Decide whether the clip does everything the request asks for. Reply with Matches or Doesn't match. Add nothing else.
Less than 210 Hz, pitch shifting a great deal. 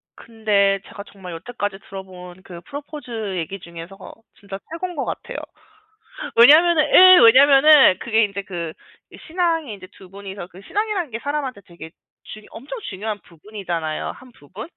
Doesn't match